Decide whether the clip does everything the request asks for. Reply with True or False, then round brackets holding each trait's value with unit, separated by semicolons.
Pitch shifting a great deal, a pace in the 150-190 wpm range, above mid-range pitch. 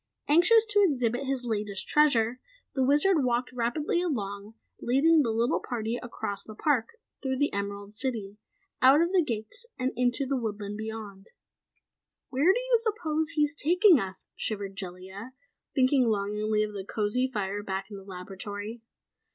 True (6.0 semitones; 160 wpm; 240 Hz)